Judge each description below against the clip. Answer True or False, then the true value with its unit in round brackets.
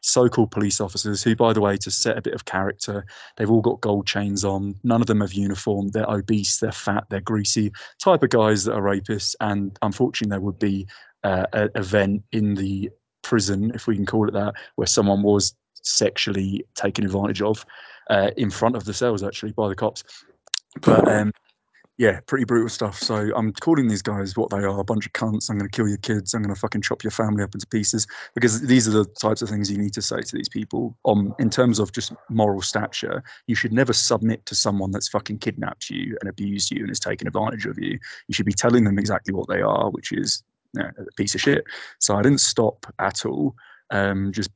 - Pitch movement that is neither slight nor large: False (2.0 semitones)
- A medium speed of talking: False (225 wpm)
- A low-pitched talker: True (105 Hz)